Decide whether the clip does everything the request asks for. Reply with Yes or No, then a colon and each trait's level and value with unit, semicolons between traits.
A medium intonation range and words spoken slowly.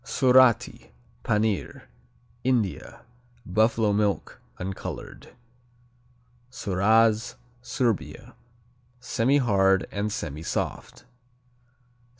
Yes: average, 3.5 semitones; slow, 55 wpm